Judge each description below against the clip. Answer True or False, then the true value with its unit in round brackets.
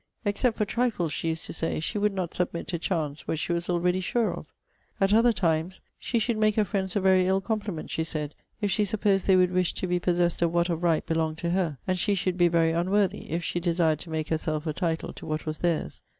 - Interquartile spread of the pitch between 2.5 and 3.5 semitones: True (3.0 semitones)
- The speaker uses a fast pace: True (250 wpm)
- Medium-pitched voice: True (175 Hz)